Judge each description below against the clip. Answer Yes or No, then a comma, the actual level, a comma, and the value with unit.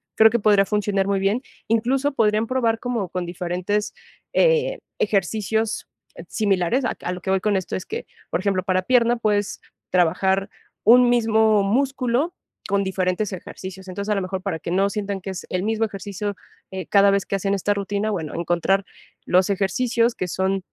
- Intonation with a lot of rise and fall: No, average, 2.9 semitones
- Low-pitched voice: No, high, 200 Hz